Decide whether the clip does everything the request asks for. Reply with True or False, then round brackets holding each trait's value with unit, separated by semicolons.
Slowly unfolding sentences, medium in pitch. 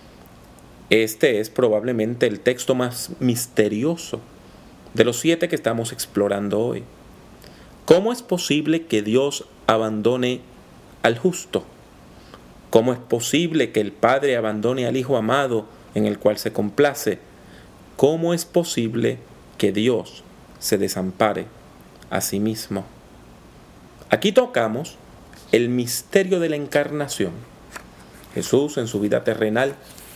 False (115 wpm; 125 Hz)